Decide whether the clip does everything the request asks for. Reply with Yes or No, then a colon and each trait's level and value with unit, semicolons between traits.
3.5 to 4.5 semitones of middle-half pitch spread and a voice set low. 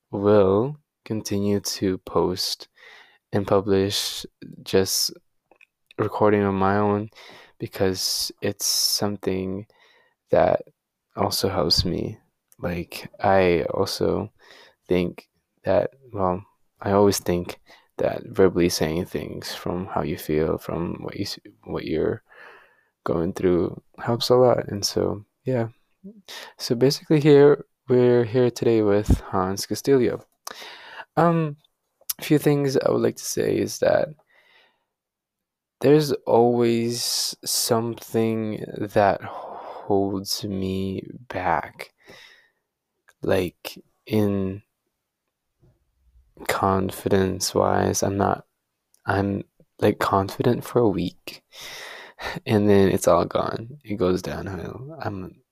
Yes: average, 4.2 semitones; low, 105 Hz